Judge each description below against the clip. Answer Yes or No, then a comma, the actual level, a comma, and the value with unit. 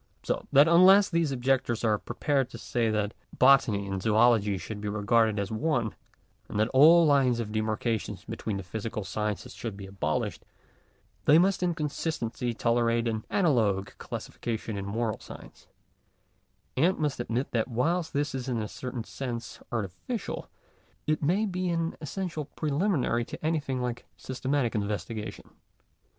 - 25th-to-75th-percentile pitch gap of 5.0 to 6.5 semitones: Yes, wide, 5.6 semitones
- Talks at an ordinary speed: Yes, average, 150 wpm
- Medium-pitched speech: No, low, 120 Hz